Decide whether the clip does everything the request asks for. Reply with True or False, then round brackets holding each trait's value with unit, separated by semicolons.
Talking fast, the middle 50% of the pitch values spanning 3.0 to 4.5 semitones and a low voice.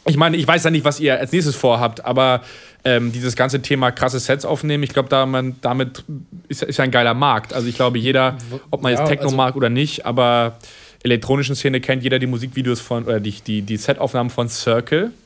False (210 wpm; 2.6 semitones; 130 Hz)